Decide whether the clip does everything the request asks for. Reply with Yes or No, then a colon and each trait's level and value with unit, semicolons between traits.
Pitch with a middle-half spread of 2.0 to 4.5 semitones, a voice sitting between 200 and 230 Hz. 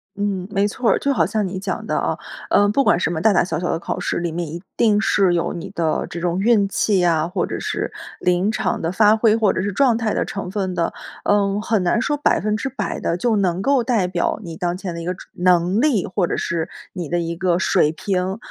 No: average, 3.5 semitones; high, 190 Hz